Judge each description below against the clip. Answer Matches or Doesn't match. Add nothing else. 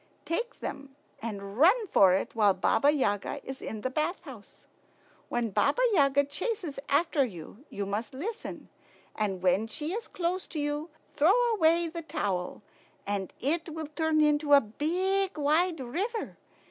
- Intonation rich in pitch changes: Matches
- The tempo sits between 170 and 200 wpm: Doesn't match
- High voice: Matches